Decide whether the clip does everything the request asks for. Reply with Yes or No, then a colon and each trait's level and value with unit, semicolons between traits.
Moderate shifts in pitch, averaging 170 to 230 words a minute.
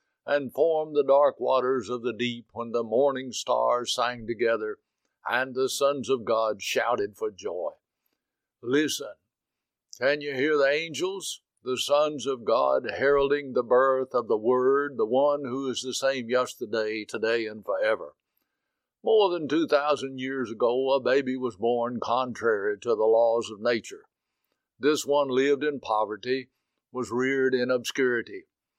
No: average, 3.4 semitones; average, 150 wpm